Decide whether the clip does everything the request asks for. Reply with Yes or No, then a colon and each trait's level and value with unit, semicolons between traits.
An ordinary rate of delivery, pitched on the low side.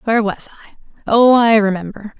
No: average, 165 wpm; high, 215 Hz